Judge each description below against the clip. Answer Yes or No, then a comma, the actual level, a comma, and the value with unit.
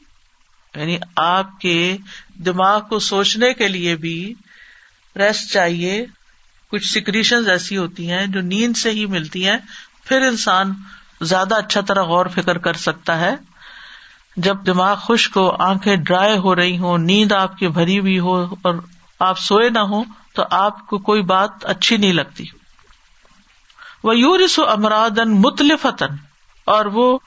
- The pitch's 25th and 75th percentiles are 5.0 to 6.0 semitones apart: No, average, 2.9 semitones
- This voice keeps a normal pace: Yes, average, 145 wpm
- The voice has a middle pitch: No, high, 195 Hz